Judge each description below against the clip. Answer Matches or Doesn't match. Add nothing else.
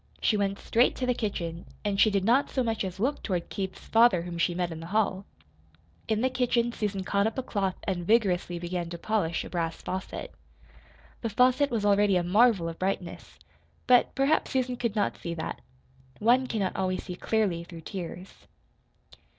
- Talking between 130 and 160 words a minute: Doesn't match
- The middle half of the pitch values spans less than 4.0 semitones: Doesn't match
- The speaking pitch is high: Matches